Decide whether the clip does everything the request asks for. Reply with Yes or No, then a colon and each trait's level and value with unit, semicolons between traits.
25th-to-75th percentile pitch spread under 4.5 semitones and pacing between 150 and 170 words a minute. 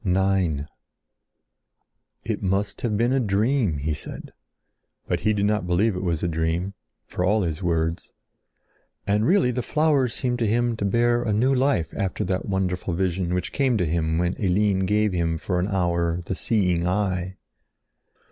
Yes: average, 4.0 semitones; average, 165 wpm